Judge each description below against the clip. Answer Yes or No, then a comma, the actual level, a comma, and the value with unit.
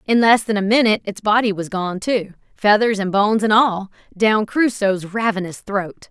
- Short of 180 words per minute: Yes, average, 165 wpm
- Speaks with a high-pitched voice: Yes, high, 210 Hz